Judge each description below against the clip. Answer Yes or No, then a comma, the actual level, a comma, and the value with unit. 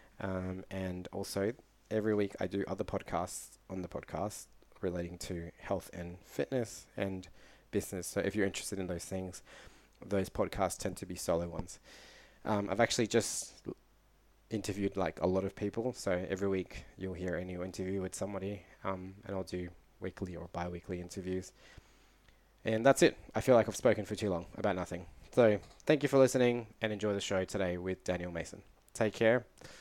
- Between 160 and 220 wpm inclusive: Yes, average, 180 wpm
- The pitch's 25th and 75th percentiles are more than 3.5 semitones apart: No, narrow, 2.4 semitones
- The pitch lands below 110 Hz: Yes, very low, 95 Hz